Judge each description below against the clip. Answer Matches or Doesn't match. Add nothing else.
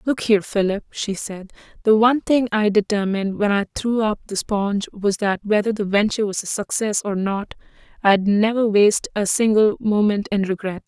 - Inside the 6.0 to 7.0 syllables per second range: Doesn't match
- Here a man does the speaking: Doesn't match